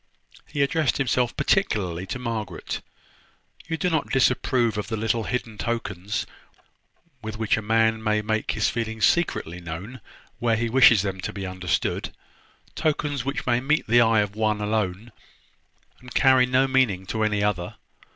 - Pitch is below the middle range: Yes, low, 110 Hz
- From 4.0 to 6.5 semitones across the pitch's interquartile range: No, average, 3.4 semitones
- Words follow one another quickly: No, average, 160 wpm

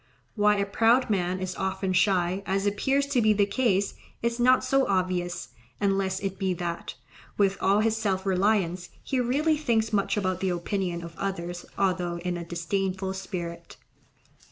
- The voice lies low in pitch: No, high, 195 Hz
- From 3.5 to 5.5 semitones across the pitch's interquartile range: No, average, 2.8 semitones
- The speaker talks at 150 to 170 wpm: Yes, average, 165 wpm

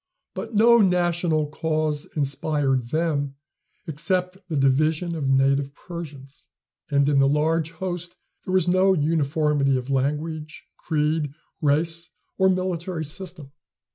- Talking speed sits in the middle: No, slow, 120 wpm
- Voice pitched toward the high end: No, medium, 155 Hz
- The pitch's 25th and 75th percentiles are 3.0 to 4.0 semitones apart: Yes, average, 3.5 semitones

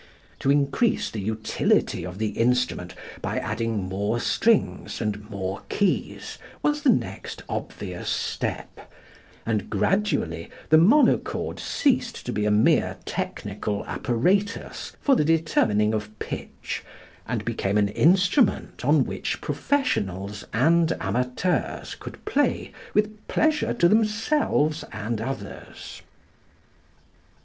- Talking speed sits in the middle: No, slow, 115 wpm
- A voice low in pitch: Yes, low, 125 Hz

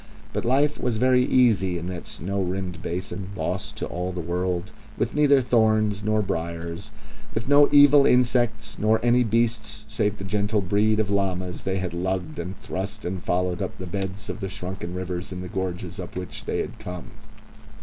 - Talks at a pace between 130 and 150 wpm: No, average, 185 wpm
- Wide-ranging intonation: No, average, 3.6 semitones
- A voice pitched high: No, very low, 95 Hz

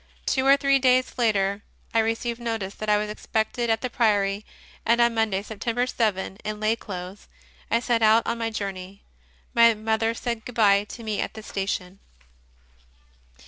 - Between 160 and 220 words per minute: Yes, average, 175 wpm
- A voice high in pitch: Yes, high, 220 Hz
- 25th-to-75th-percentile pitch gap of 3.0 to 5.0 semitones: No, narrow, 2.5 semitones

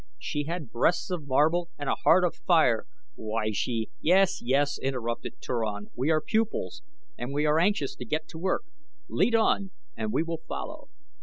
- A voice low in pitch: No, medium, 150 Hz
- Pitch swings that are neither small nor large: No, wide, 6.2 semitones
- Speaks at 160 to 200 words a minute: Yes, average, 180 wpm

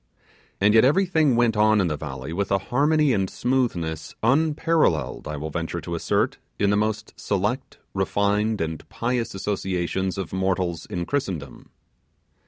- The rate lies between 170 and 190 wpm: No, average, 150 wpm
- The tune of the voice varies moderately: No, wide, 6.0 semitones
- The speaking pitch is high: No, low, 100 Hz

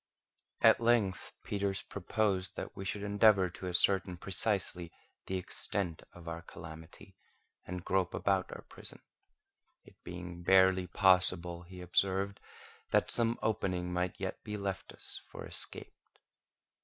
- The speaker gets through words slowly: Yes, slow, 130 wpm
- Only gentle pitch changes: Yes, narrow, 2.0 semitones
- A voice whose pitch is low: Yes, very low, 95 Hz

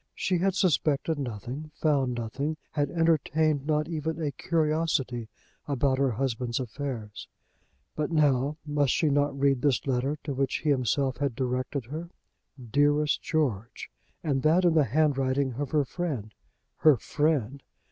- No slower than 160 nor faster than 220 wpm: No, average, 145 wpm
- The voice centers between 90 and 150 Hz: Yes, medium, 140 Hz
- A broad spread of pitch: No, average, 3.0 semitones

